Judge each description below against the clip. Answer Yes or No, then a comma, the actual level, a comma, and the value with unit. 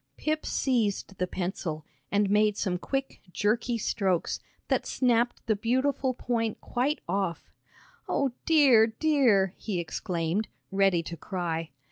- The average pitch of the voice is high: Yes, high, 210 Hz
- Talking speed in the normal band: No, slow, 125 wpm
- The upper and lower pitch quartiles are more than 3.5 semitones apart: Yes, average, 5.2 semitones